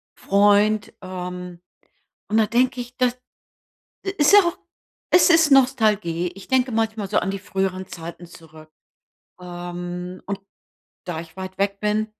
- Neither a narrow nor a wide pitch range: Yes, average, 3.9 semitones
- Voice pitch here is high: Yes, high, 195 Hz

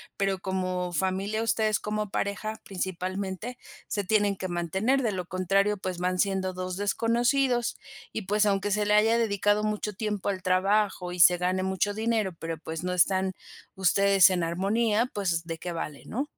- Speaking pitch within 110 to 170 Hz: No, high, 195 Hz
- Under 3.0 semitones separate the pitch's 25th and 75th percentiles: Yes, narrow, 2.5 semitones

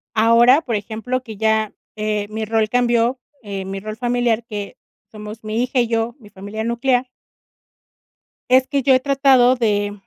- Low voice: No, high, 225 Hz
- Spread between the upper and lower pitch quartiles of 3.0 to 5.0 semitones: No, narrow, 2.5 semitones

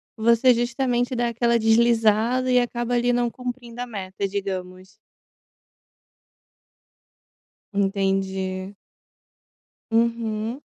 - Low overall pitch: No, high, 230 Hz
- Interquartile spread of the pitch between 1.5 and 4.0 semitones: Yes, average, 3.4 semitones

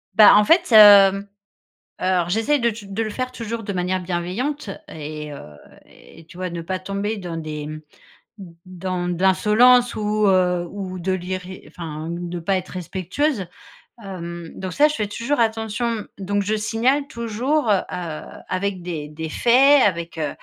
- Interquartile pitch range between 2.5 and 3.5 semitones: No, average, 4.2 semitones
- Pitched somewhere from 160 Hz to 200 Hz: Yes, high, 190 Hz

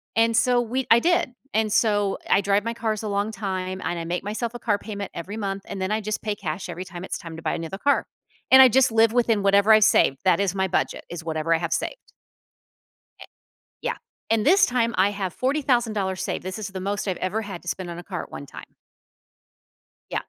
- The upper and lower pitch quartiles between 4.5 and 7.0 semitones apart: No, average, 3.3 semitones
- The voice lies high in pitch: Yes, high, 205 Hz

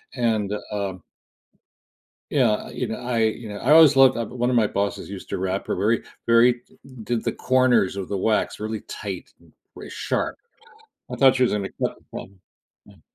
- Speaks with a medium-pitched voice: No, low, 110 Hz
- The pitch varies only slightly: No, average, 3.7 semitones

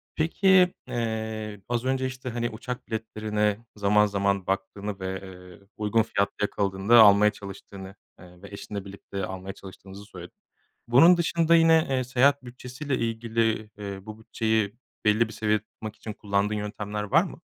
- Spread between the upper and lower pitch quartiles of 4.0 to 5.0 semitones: No, average, 3.0 semitones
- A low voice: Yes, low, 105 Hz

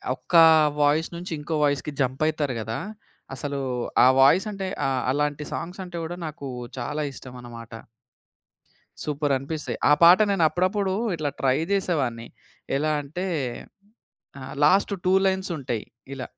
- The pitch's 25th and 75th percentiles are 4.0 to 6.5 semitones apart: Yes, average, 4.5 semitones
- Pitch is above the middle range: No, medium, 150 Hz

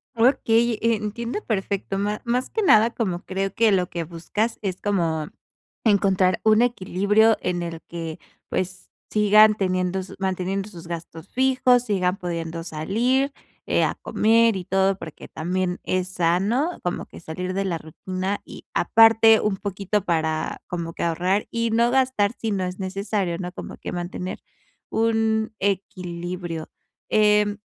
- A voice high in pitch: Yes, high, 195 Hz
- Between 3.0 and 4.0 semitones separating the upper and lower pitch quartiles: Yes, average, 3.7 semitones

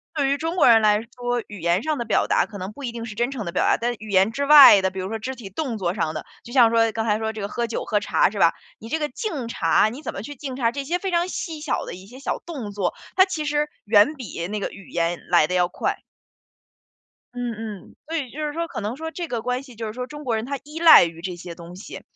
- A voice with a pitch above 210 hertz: Yes, high, 230 Hz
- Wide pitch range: Yes, wide, 5.7 semitones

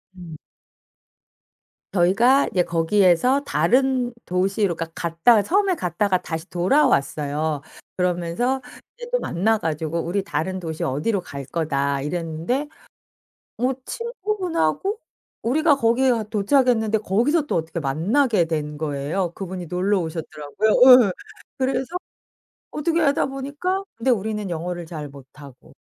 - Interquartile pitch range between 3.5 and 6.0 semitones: No, wide, 7.9 semitones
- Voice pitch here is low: No, high, 190 Hz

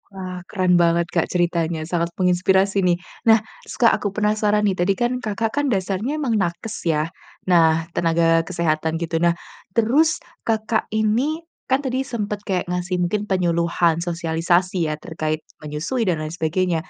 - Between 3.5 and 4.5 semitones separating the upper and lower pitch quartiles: Yes, average, 4.0 semitones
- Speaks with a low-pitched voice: No, medium, 180 Hz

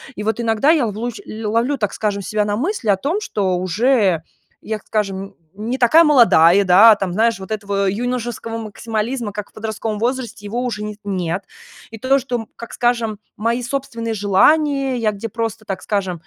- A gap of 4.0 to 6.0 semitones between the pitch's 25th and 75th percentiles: No, average, 3.0 semitones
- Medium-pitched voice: No, high, 220 Hz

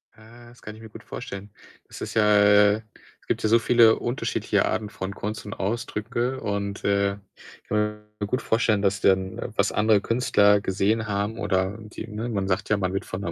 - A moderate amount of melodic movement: No, narrow, 1.8 semitones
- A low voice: Yes, low, 105 Hz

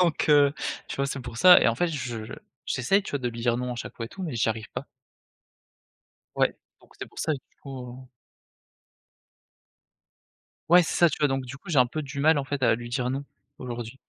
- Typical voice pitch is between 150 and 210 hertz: No, low, 135 Hz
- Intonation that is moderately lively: Yes, average, 3.4 semitones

